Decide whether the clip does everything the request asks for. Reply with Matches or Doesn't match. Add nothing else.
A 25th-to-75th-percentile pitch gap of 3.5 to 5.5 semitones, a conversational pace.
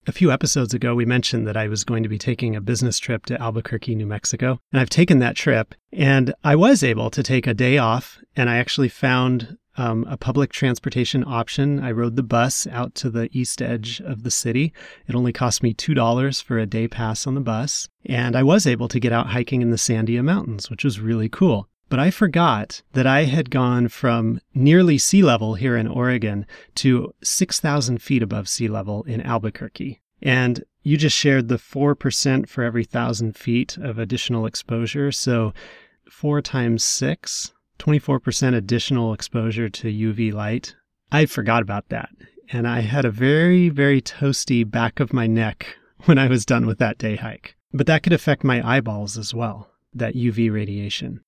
Doesn't match